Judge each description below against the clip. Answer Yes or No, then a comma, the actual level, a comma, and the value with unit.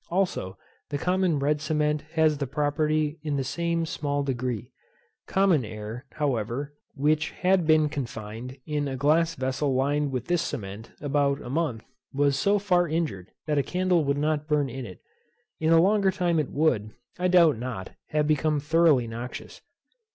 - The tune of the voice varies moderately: Yes, average, 3.7 semitones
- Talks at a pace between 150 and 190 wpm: Yes, average, 165 wpm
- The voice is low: No, medium, 150 Hz